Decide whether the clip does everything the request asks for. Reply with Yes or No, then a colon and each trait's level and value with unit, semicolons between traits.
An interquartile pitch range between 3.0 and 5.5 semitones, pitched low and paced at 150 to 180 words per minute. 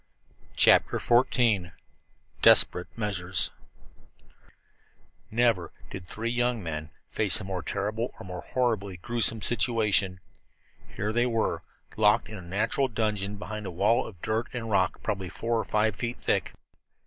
No: average, 3.5 semitones; low, 105 Hz; slow, 135 wpm